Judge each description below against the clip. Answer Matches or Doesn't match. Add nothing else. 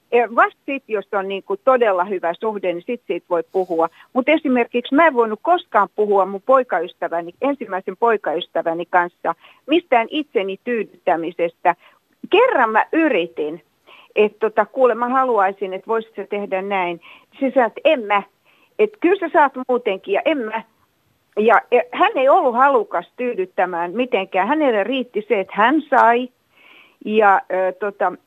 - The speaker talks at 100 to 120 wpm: Doesn't match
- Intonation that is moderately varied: Doesn't match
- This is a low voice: Doesn't match